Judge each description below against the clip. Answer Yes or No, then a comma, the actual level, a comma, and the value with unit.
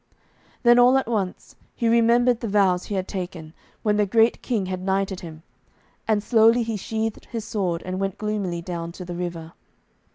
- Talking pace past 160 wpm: Yes, average, 185 wpm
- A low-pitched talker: No, high, 200 Hz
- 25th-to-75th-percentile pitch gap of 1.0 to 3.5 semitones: No, average, 3.9 semitones